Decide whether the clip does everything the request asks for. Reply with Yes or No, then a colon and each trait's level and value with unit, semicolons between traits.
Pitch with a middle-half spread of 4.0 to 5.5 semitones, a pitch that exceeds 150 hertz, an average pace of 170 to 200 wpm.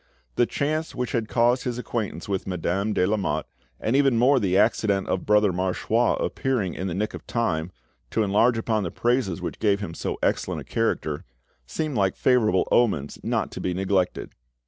No: average, 4.3 semitones; low, 105 Hz; average, 185 wpm